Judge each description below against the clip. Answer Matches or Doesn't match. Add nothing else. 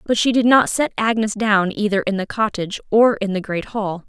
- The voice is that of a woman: Matches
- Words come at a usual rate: Doesn't match